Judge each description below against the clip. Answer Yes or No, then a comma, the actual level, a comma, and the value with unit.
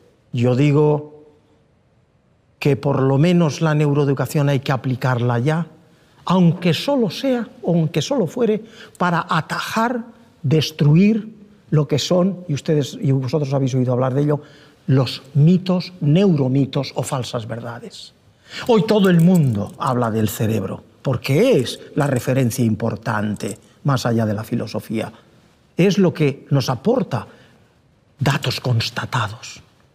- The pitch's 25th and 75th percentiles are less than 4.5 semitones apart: No, average, 5.1 semitones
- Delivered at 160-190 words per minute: No, average, 130 wpm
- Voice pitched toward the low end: No, medium, 145 Hz